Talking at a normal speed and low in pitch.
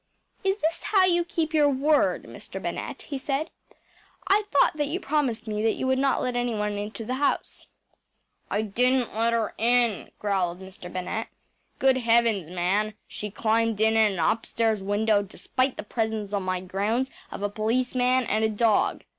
No: average, 175 wpm; high, 225 Hz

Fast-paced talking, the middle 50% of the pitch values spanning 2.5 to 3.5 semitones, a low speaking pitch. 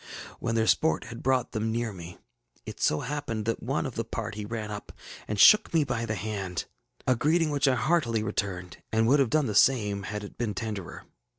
No: fast, 210 wpm; average, 3.9 semitones; low, 115 Hz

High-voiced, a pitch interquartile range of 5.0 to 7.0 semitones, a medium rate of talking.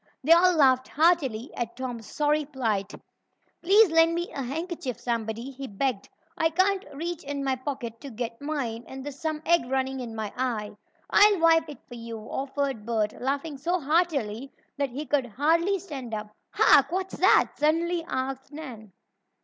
Yes: very high, 275 Hz; average, 5.3 semitones; average, 170 wpm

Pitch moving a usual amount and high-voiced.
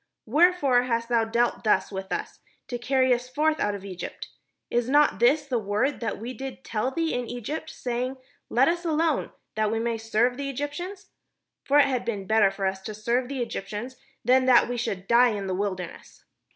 Yes: average, 3.8 semitones; high, 245 Hz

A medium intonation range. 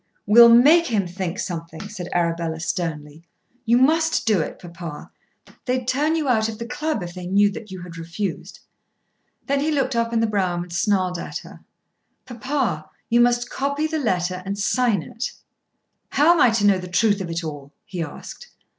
No: wide, 6.0 semitones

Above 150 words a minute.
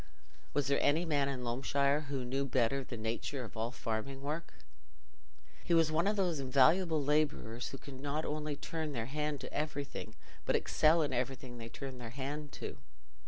Yes: average, 180 wpm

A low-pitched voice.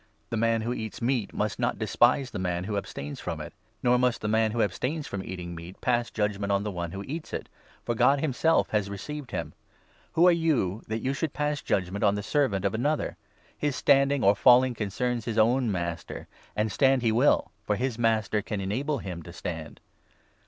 Yes: low, 110 Hz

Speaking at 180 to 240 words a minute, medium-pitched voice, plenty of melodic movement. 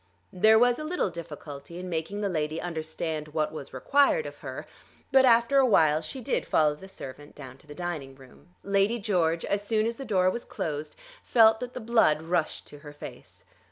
Yes: average, 200 wpm; medium, 175 Hz; wide, 6.4 semitones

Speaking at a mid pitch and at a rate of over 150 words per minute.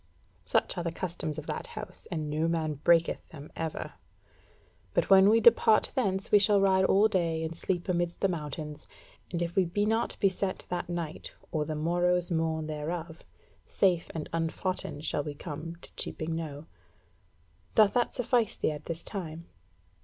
Yes: medium, 170 Hz; average, 175 wpm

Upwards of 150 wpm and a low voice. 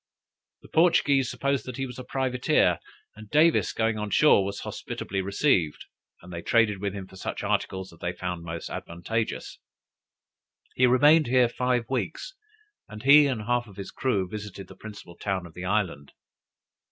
Yes: average, 170 wpm; low, 105 Hz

